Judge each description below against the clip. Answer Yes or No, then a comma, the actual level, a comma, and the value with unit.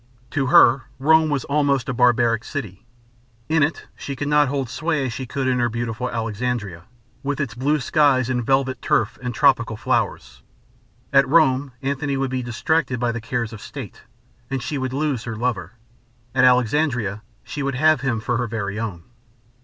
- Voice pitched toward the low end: Yes, low, 130 Hz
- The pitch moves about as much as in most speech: Yes, average, 3.3 semitones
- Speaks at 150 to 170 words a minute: No, average, 180 wpm